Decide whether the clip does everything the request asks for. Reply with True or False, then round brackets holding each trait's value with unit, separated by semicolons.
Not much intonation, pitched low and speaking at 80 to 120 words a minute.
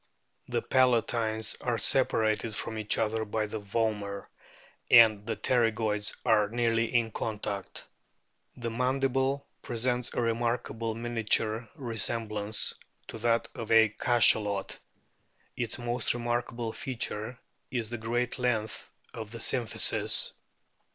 True (1.8 semitones; 115 Hz; 115 wpm)